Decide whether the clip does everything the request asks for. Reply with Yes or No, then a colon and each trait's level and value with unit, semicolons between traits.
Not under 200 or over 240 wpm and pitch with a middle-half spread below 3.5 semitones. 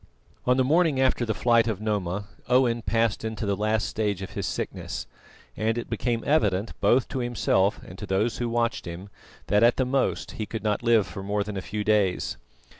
Yes: fast, 205 wpm; average, 2.8 semitones